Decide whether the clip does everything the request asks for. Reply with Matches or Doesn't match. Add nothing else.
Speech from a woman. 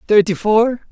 Doesn't match